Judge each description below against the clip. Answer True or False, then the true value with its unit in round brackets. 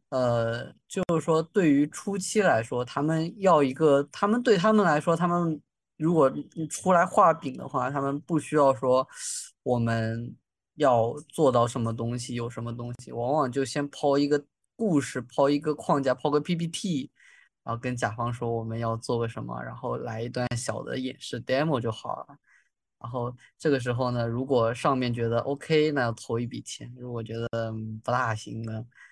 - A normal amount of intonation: True (4.4 semitones)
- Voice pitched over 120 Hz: True (130 Hz)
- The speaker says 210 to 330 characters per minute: True (265 characters per minute)